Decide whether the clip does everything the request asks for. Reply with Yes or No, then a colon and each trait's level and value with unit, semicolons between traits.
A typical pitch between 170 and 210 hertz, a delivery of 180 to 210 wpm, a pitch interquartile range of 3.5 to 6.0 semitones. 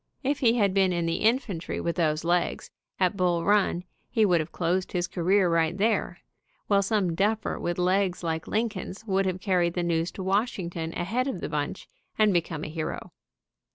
No: medium, 185 Hz; average, 190 wpm; average, 3.1 semitones